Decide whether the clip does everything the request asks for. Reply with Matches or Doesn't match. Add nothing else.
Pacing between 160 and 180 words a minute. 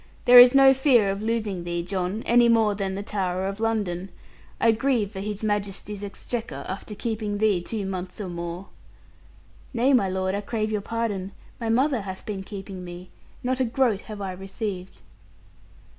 Matches